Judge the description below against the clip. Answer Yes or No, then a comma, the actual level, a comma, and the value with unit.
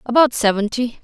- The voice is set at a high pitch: Yes, high, 235 Hz